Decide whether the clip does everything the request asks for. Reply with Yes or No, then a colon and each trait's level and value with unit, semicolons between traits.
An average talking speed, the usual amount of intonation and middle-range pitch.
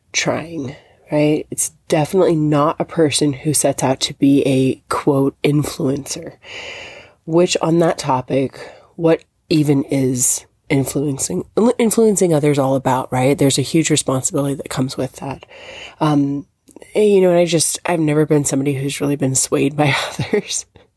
Yes: average, 150 wpm; average, 3.2 semitones; medium, 145 Hz